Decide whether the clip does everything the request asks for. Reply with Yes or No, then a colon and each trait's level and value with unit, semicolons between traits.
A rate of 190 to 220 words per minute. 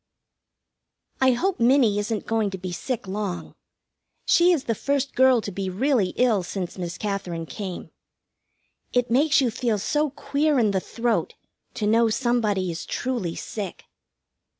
No: average, 150 wpm